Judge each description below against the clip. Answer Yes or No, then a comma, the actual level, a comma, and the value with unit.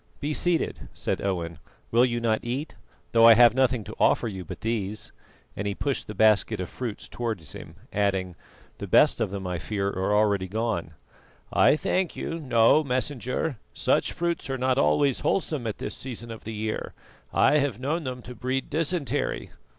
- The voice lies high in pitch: No, low, 115 Hz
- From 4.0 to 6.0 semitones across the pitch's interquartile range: Yes, average, 4.7 semitones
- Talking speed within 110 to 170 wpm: No, average, 180 wpm